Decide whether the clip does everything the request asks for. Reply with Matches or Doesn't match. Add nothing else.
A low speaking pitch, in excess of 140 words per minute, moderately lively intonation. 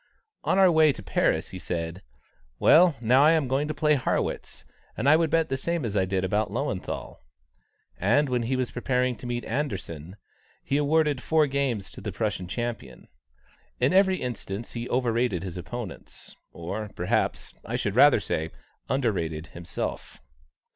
Doesn't match